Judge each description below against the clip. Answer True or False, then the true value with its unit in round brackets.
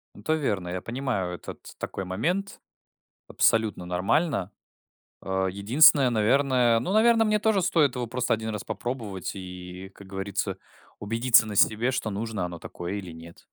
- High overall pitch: False (110 Hz)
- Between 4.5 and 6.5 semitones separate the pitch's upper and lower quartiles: True (5.6 semitones)